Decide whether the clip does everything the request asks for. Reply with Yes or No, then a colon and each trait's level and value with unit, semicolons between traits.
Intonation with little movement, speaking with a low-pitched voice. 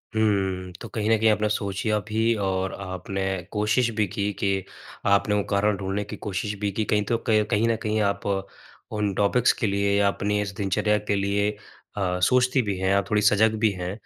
Yes: narrow, 1.5 semitones; low, 105 Hz